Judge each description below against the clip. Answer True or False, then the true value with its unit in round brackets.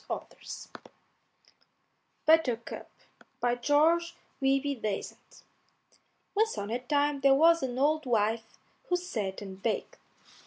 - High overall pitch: True (270 Hz)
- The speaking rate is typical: False (105 wpm)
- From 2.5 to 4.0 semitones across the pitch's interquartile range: False (5.3 semitones)